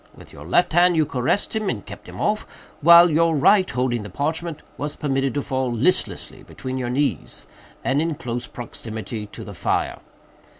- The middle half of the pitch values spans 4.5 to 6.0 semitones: Yes, wide, 5.4 semitones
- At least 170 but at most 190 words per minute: Yes, average, 180 wpm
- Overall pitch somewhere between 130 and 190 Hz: Yes, medium, 140 Hz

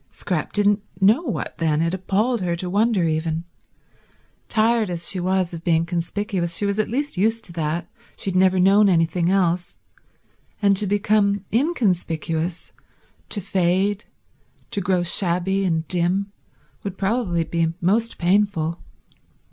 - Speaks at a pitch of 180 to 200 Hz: Yes, high, 190 Hz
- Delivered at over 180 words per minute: No, average, 145 wpm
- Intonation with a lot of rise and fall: No, average, 3.2 semitones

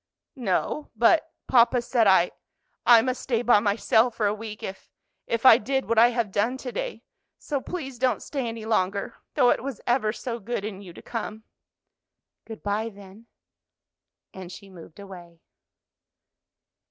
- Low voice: No, high, 225 Hz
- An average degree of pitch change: Yes, average, 3.4 semitones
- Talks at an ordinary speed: Yes, average, 165 wpm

